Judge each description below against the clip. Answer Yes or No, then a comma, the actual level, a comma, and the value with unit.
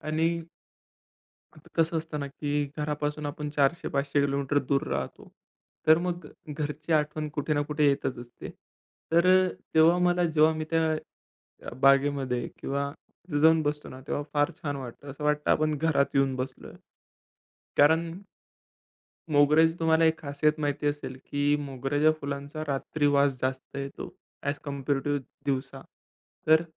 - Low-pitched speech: No, medium, 145 Hz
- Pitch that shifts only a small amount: Yes, narrow, 2.0 semitones